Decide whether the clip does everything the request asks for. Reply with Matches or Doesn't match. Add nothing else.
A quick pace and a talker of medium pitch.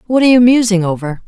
Doesn't match